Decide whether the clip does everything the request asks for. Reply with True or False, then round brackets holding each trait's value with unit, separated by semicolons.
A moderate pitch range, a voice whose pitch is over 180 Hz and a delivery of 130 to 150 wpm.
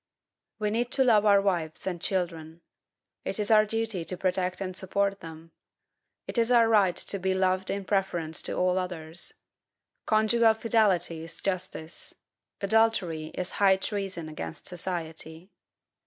True (3.6 semitones; 190 Hz; 145 wpm)